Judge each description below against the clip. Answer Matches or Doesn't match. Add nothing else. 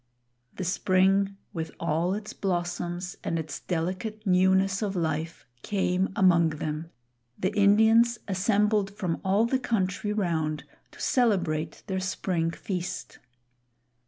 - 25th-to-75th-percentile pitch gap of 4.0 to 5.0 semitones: Doesn't match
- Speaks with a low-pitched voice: Doesn't match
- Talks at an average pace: Doesn't match